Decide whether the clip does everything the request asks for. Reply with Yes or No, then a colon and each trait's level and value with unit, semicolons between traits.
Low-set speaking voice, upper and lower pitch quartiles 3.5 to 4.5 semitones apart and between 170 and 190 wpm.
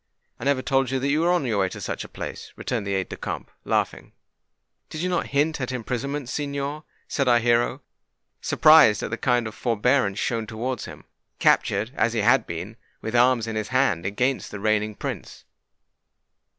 Yes: low, 120 Hz; average, 4.1 semitones; average, 185 wpm